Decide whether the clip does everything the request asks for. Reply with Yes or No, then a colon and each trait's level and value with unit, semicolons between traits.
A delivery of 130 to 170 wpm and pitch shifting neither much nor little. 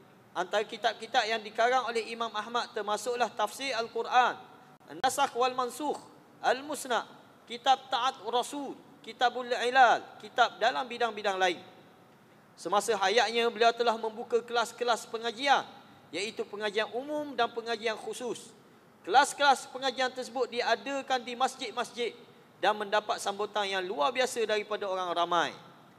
No: average, 120 wpm; average, 3.5 semitones